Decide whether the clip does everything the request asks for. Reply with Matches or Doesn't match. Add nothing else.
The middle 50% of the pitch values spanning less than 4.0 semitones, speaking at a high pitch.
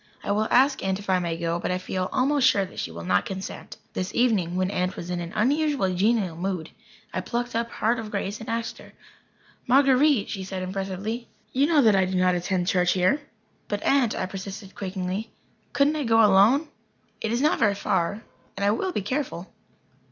Doesn't match